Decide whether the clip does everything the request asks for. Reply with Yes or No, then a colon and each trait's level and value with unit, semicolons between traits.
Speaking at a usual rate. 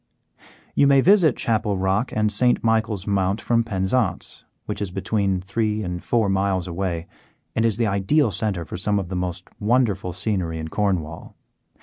Yes: average, 165 wpm